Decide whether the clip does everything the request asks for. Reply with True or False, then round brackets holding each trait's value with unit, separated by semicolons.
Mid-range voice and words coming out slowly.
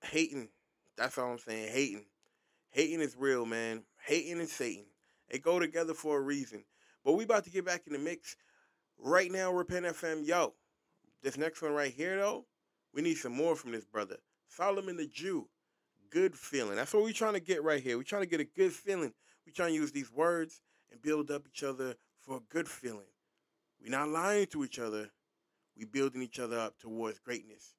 False (155 Hz; 205 wpm)